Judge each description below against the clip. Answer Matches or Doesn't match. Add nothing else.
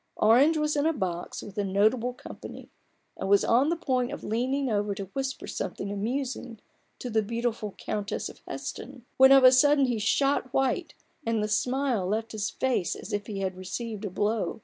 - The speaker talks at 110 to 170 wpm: Doesn't match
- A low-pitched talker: Doesn't match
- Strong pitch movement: Doesn't match